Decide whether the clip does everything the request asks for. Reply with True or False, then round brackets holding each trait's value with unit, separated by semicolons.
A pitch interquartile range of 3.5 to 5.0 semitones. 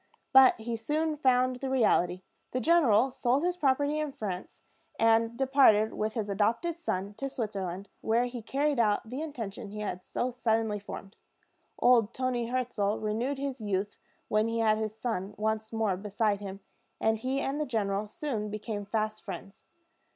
True (3.8 semitones)